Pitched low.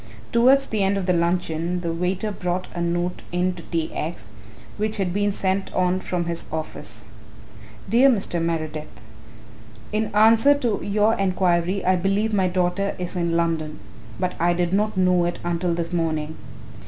No: medium, 180 Hz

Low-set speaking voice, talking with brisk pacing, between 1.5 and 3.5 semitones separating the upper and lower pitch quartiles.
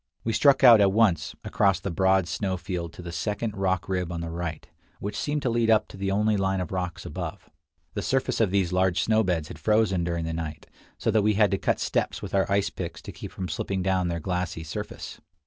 Yes: very low, 95 Hz; fast, 235 wpm; average, 3.2 semitones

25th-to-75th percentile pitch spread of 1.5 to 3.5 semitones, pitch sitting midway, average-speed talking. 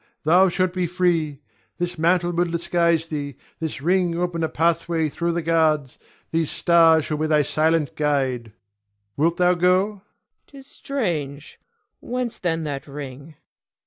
Yes: narrow, 2.6 semitones; medium, 165 Hz; average, 145 wpm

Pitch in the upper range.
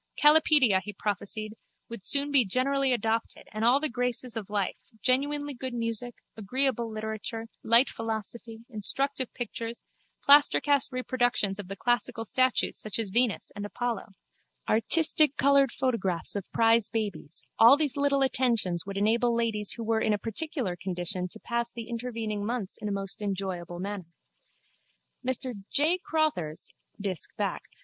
Yes: high, 230 Hz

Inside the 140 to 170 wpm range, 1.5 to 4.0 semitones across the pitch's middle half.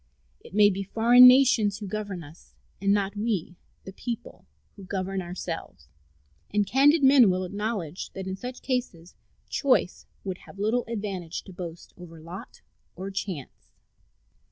Yes: average, 155 wpm; average, 3.7 semitones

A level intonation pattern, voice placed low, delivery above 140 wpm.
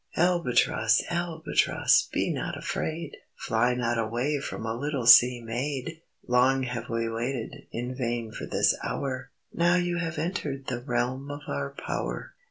No: average, 4.1 semitones; low, 125 Hz; average, 150 wpm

